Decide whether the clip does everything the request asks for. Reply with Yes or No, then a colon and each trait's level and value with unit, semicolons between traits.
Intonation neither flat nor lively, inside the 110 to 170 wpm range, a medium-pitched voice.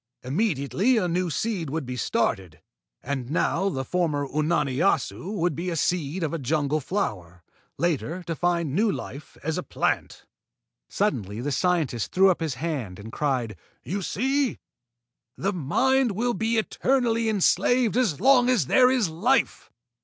No: wide, 7.1 semitones; average, 155 wpm; medium, 170 Hz